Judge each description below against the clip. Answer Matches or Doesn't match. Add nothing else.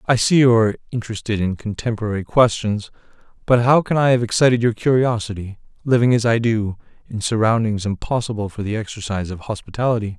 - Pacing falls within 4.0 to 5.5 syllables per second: Doesn't match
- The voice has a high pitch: Doesn't match